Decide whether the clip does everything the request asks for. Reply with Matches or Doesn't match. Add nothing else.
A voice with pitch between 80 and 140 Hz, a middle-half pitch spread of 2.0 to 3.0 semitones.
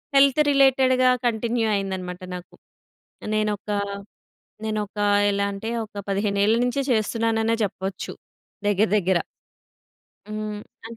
Doesn't match